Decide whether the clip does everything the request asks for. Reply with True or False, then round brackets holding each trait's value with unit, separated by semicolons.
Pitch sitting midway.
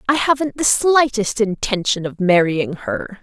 False (220 Hz)